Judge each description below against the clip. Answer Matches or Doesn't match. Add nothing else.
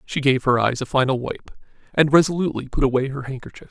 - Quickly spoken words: Matches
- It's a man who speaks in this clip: Matches